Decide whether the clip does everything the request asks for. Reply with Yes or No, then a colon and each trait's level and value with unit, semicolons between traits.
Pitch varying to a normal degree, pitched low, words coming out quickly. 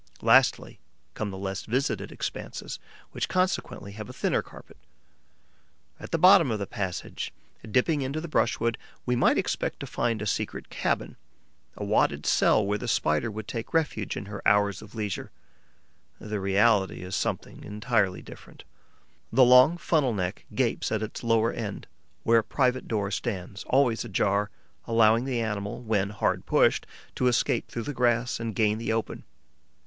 No: average, 3.3 semitones; low, 110 Hz; average, 165 wpm